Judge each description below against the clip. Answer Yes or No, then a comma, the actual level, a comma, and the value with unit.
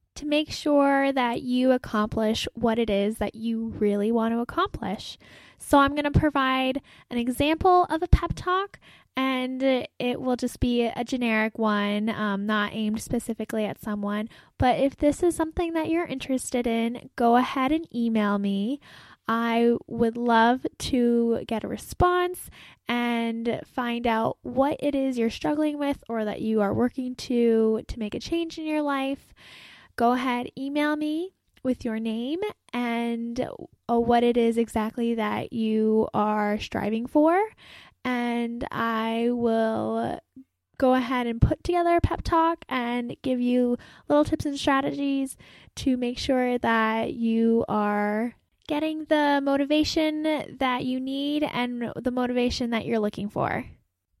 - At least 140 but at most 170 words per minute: Yes, average, 150 wpm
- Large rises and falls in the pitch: No, average, 3.6 semitones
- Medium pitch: No, high, 245 Hz